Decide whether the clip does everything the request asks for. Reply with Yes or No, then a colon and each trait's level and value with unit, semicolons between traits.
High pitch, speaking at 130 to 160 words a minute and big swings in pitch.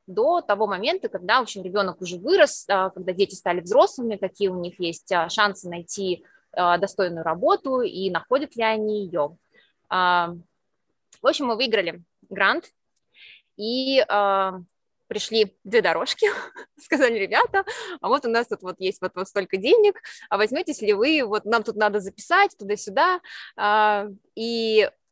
Yes: high, 210 Hz; average, 135 wpm; wide, 7.3 semitones